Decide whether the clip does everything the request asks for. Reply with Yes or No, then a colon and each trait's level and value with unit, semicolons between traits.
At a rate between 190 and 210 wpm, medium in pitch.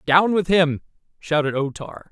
No: average, 170 wpm; medium, 165 Hz